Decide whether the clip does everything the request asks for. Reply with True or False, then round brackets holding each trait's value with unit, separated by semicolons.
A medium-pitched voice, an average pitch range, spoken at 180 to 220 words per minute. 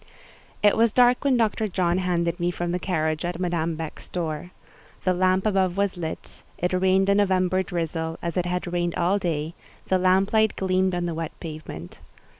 False (180 Hz; 1.9 semitones; 185 wpm)